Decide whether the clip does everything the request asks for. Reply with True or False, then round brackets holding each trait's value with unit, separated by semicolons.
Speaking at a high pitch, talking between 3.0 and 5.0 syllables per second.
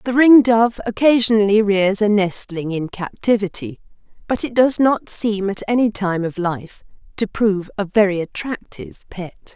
True (205 Hz; 4.7 syllables/s)